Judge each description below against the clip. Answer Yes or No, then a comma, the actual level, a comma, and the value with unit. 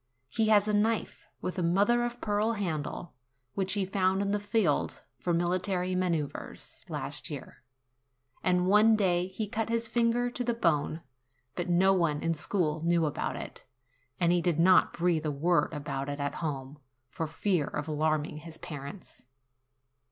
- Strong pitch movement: No, average, 4.5 semitones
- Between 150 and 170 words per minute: Yes, average, 165 wpm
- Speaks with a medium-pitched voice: Yes, medium, 180 Hz